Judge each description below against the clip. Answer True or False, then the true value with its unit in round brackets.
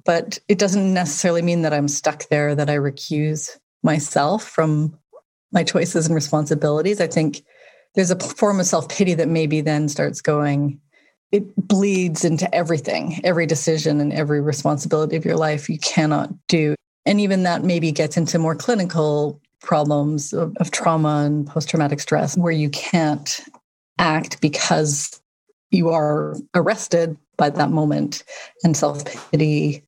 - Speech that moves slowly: False (155 wpm)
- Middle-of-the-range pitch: True (160 Hz)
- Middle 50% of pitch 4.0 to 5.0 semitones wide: False (2.5 semitones)